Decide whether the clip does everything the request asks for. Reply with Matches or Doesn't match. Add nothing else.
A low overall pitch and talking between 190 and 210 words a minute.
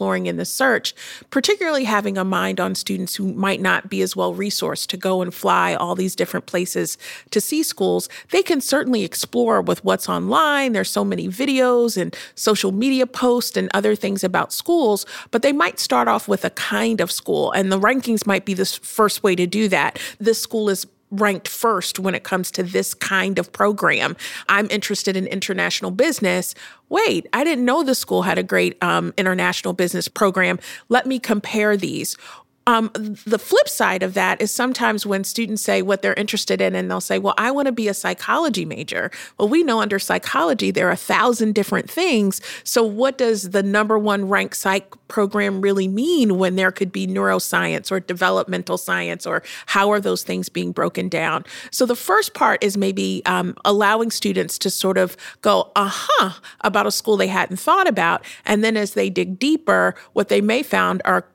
Doesn't match